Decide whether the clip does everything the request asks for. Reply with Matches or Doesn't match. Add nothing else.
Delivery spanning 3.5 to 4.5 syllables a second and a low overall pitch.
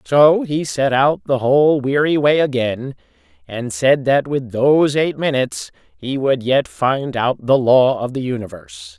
Matches